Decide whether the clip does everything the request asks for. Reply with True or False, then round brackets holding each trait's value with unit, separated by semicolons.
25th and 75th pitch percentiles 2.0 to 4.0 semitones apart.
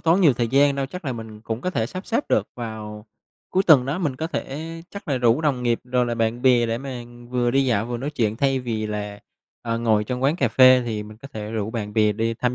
True (3.7 semitones)